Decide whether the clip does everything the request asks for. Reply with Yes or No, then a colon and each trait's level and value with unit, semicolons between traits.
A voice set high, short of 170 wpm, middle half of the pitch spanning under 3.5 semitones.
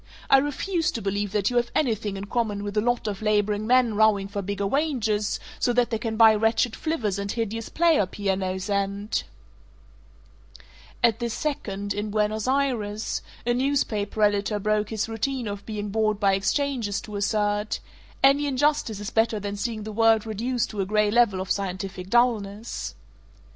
No: high, 215 Hz; average, 175 wpm; average, 2.8 semitones